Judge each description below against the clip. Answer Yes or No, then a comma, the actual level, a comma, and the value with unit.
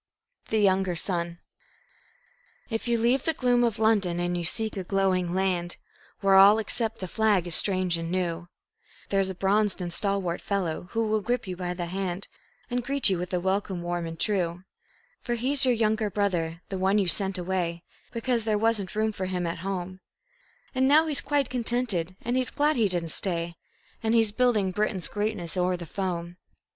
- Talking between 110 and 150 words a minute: No, average, 190 wpm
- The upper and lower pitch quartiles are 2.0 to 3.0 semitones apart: No, average, 4.0 semitones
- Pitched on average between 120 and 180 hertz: No, high, 195 Hz